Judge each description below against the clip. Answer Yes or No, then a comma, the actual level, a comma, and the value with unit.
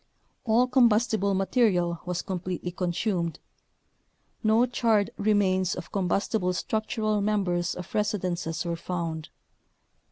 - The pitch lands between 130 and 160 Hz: No, high, 190 Hz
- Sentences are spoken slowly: Yes, slow, 100 wpm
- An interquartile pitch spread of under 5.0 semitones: Yes, average, 3.4 semitones